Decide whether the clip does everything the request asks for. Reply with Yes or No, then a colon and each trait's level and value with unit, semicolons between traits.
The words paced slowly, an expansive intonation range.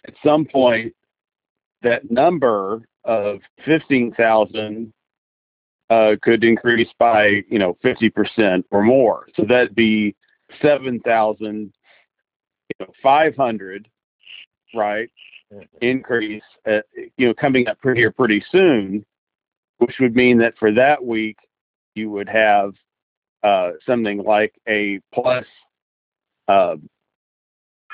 No: slow, 105 wpm; average, 2.9 semitones